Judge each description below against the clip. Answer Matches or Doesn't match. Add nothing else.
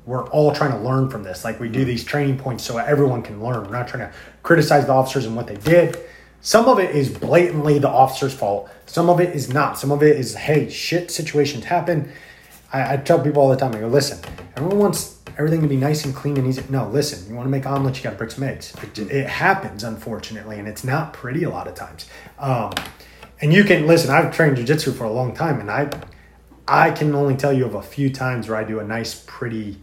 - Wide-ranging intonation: Doesn't match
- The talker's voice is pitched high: Doesn't match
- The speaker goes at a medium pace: Doesn't match